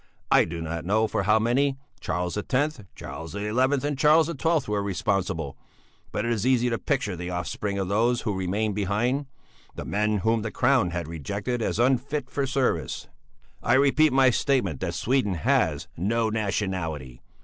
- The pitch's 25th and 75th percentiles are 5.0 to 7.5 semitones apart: Yes, wide, 5.5 semitones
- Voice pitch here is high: No, low, 110 Hz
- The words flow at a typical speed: Yes, average, 170 wpm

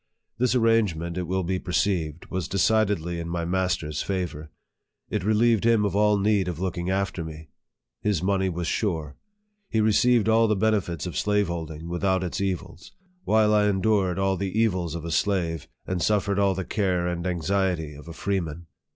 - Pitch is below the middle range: Yes, very low, 95 Hz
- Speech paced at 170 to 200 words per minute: Yes, average, 175 wpm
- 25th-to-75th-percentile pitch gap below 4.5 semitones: Yes, average, 3.3 semitones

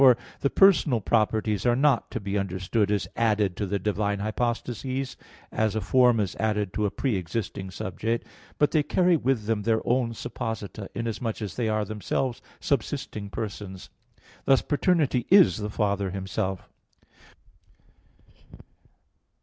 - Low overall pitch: Yes, low, 110 Hz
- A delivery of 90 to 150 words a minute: Yes, average, 140 wpm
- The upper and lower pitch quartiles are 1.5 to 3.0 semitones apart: No, average, 3.4 semitones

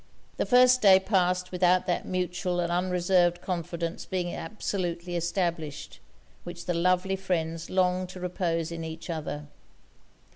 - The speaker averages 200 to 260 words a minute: No, slow, 135 wpm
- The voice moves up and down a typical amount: No, narrow, 1.4 semitones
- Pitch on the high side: No, medium, 180 Hz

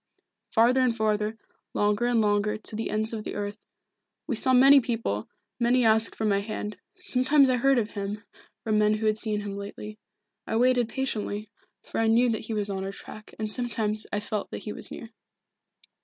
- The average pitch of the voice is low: No, high, 220 Hz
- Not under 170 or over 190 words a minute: No, average, 200 wpm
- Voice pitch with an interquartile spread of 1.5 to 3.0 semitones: Yes, narrow, 2.4 semitones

